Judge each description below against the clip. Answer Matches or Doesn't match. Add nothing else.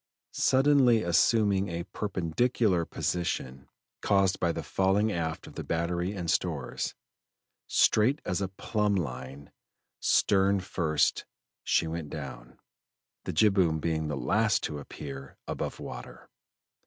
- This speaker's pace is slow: Matches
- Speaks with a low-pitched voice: Matches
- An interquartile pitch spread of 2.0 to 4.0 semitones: Doesn't match